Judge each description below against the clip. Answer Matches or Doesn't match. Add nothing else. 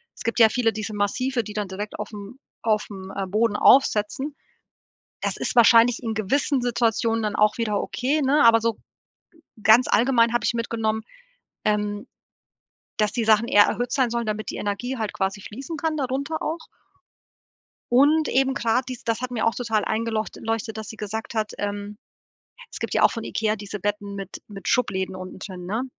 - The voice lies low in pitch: Doesn't match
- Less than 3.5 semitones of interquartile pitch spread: Matches